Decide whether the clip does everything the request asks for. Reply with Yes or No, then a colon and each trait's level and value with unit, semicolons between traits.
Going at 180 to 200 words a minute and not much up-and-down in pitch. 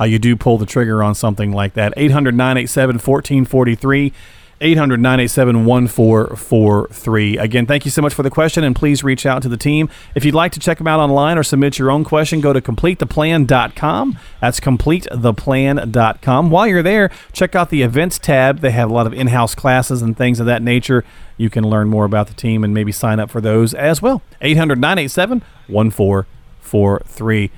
No: average, 190 wpm; average, 4.5 semitones